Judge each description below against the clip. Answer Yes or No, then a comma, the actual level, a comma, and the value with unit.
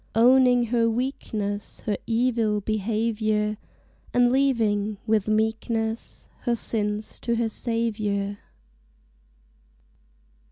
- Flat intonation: Yes, narrow, 1.9 semitones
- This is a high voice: Yes, high, 220 Hz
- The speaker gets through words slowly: Yes, slow, 85 wpm